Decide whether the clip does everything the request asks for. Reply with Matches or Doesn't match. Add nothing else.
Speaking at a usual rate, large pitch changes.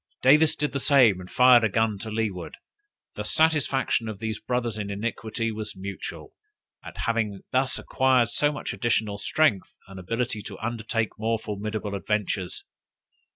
Doesn't match